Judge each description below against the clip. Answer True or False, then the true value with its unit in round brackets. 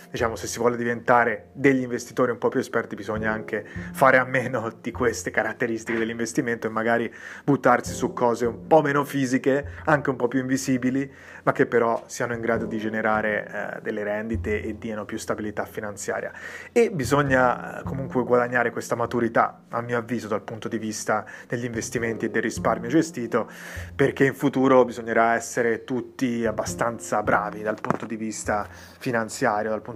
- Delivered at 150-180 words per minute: True (170 wpm)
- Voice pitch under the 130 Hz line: True (115 Hz)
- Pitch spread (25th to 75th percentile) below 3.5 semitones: True (2.8 semitones)